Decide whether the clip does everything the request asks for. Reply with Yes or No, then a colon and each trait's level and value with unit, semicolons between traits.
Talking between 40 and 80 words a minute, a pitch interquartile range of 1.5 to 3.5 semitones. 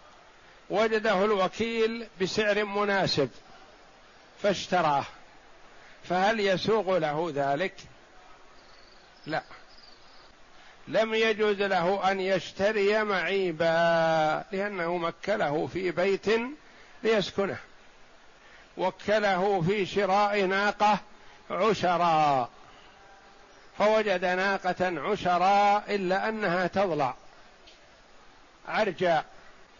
Yes: slow, 65 wpm; narrow, 2.4 semitones